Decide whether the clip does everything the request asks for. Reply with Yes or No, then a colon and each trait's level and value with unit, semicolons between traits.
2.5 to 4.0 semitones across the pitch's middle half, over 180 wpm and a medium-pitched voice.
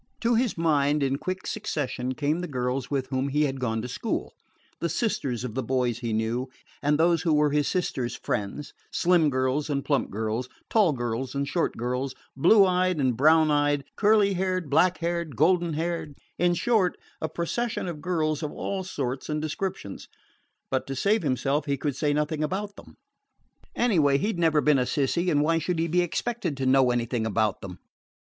No: average, 4.9 semitones; average, 190 wpm; medium, 150 Hz